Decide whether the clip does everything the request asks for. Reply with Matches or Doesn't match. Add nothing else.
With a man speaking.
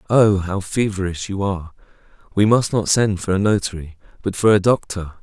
Matches